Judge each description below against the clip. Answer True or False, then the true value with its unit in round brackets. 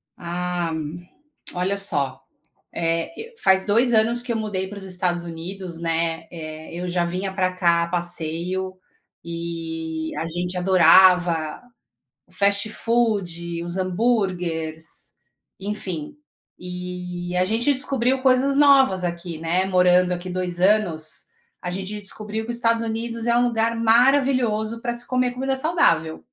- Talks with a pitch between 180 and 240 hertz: True (185 Hz)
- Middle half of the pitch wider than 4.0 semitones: True (4.7 semitones)